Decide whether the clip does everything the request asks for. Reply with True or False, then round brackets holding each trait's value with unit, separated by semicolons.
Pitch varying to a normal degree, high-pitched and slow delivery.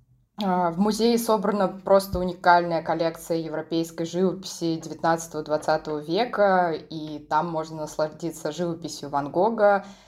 False (3.1 semitones; 165 Hz; 100 wpm)